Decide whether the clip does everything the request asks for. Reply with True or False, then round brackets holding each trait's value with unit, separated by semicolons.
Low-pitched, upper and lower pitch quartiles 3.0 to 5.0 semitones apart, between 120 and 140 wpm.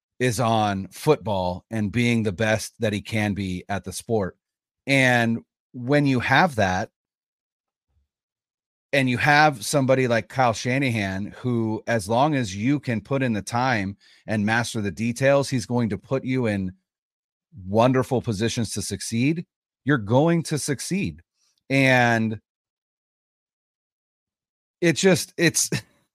True (115 Hz; 4.2 semitones; 135 wpm)